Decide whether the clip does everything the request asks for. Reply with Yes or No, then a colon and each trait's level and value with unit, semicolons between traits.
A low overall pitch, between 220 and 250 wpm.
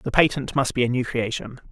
Yes: low, 130 Hz; fast, 245 wpm